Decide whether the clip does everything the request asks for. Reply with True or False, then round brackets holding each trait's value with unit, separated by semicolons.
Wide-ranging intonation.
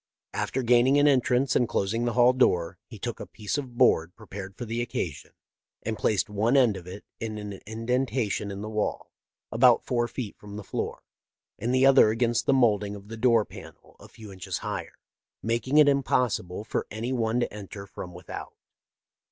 False (3.4 semitones)